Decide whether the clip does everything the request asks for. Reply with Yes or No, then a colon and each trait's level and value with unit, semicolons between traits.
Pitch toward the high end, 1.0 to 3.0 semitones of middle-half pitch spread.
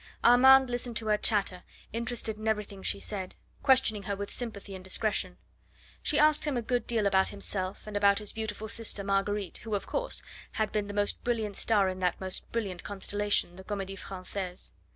Yes: high, 205 Hz; narrow, 2.6 semitones